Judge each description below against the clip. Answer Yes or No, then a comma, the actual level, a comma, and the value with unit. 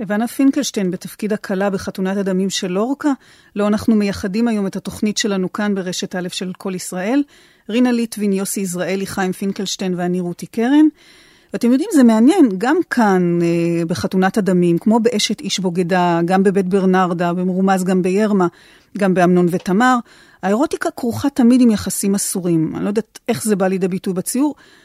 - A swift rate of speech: Yes, fast, 160 wpm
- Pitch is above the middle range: Yes, high, 200 Hz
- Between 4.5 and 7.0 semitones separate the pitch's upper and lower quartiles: No, average, 4.0 semitones